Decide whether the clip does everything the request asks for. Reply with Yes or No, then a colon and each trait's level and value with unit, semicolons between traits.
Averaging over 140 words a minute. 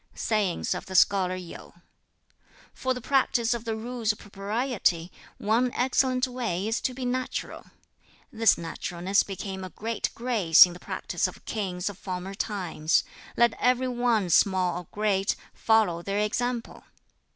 Yes: average, 150 wpm